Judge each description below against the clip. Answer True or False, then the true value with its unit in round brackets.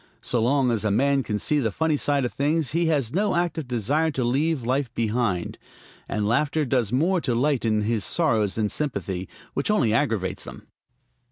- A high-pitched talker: False (130 Hz)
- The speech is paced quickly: False (185 wpm)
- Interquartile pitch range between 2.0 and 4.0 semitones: False (5.2 semitones)